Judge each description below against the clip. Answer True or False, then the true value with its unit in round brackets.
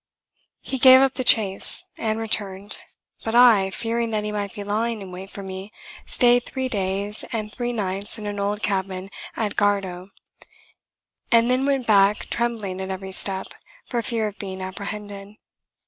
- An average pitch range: True (3.1 semitones)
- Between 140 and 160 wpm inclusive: False (170 wpm)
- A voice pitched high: True (205 Hz)